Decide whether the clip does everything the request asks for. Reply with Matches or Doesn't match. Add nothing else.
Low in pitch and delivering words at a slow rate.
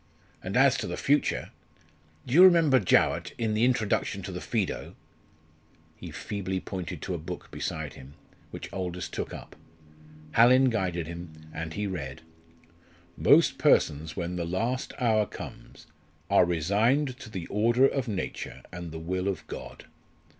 Doesn't match